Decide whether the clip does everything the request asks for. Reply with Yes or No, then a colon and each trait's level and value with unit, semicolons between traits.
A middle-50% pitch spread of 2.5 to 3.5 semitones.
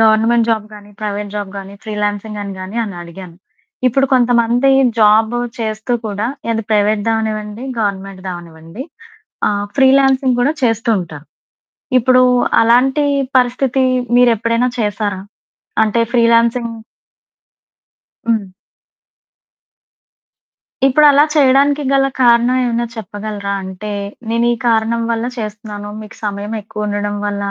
Yes: average, 2.8 semitones